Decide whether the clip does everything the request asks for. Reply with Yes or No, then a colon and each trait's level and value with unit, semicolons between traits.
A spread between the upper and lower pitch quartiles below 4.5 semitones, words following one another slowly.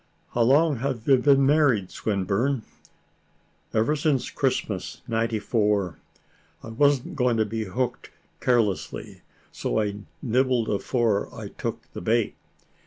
Yes: average, 3.7 semitones; slow, 120 wpm